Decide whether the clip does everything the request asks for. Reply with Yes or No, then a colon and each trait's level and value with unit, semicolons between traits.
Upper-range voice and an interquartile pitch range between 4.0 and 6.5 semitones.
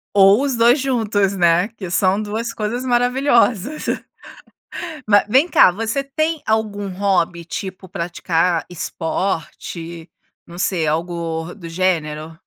Yes: high, 195 Hz; average, 5.2 semitones